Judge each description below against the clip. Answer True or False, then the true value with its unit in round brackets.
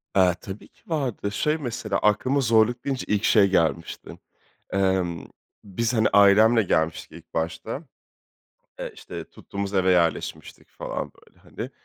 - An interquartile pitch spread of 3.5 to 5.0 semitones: True (4.0 semitones)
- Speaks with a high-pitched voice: False (100 Hz)